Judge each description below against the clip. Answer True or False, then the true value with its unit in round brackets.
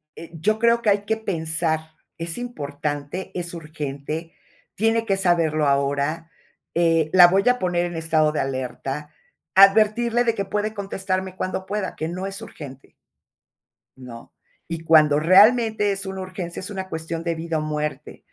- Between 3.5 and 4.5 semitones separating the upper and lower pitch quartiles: True (4.1 semitones)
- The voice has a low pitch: False (170 Hz)